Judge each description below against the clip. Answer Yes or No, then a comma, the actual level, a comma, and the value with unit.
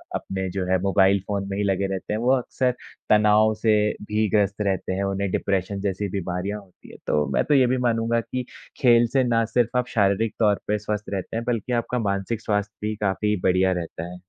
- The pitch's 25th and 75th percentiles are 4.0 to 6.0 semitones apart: No, average, 2.9 semitones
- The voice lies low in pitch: Yes, low, 105 Hz